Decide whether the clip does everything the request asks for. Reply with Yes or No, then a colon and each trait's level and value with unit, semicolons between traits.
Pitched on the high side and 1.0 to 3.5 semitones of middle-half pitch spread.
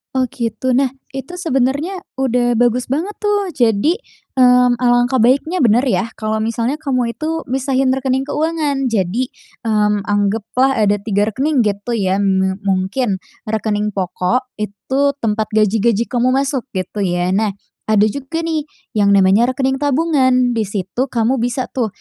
No: high, 245 Hz; average, 4.3 semitones